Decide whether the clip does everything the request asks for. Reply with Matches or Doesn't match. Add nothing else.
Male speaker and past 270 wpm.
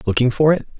Doesn't match